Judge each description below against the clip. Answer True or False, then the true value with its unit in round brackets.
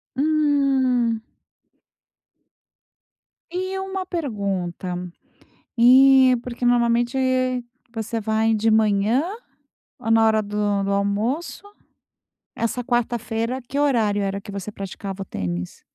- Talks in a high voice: True (225 Hz)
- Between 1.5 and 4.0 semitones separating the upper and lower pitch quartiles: False (4.4 semitones)